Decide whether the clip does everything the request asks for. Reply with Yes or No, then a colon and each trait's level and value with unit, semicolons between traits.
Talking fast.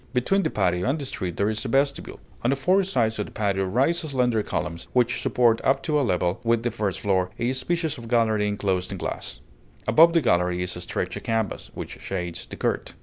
Yes: fast, 220 wpm